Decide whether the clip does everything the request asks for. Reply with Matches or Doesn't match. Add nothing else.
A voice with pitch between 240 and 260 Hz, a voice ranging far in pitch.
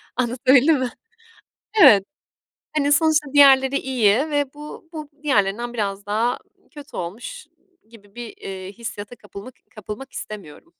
Matches